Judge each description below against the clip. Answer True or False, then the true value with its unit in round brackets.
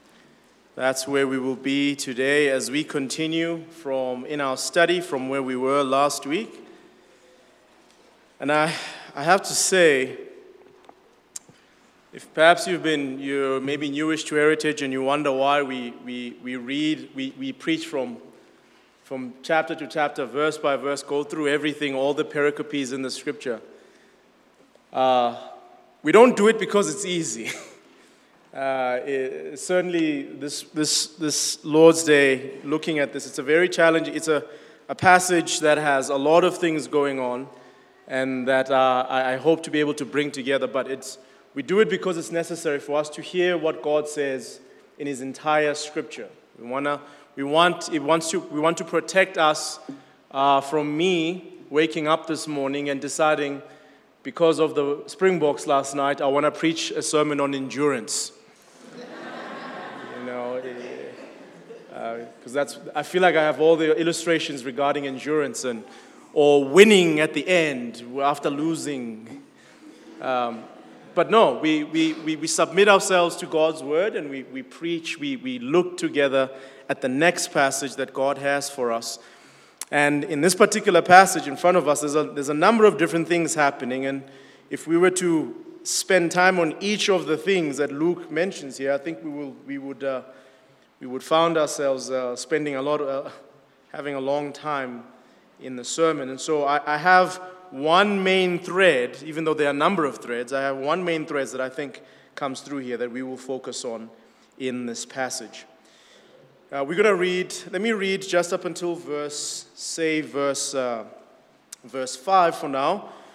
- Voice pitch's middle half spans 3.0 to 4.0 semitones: True (3.6 semitones)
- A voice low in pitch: False (150 Hz)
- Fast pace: False (175 wpm)